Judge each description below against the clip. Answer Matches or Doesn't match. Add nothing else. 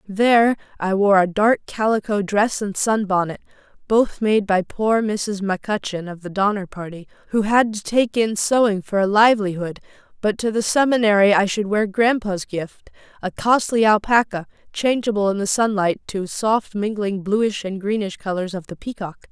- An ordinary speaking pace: Matches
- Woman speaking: Matches